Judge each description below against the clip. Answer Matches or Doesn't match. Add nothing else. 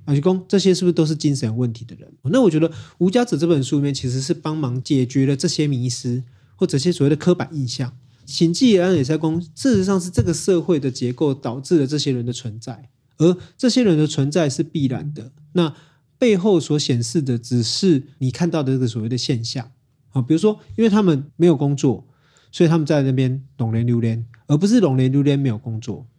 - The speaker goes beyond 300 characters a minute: Matches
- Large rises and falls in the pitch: Doesn't match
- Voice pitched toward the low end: Doesn't match